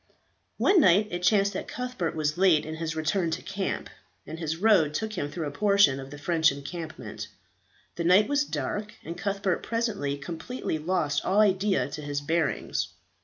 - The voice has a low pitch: No, medium, 170 Hz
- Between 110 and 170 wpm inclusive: No, average, 180 wpm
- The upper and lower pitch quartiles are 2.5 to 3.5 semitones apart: No, average, 4.9 semitones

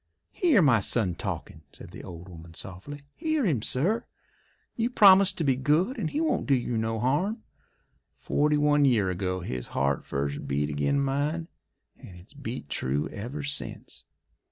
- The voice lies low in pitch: Yes, low, 130 Hz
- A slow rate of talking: No, average, 165 wpm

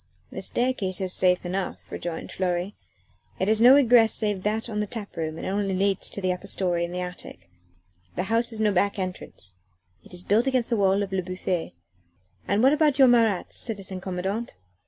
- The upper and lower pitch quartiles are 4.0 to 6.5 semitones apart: No, average, 3.5 semitones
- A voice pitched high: Yes, high, 195 Hz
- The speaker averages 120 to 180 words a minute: No, average, 200 wpm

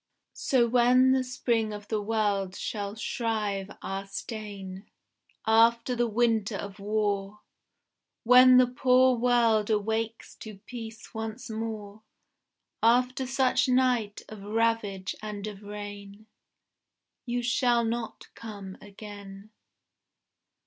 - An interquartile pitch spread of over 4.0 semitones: No, average, 2.8 semitones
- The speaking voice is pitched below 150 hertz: No, high, 220 Hz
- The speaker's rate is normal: No, slow, 110 wpm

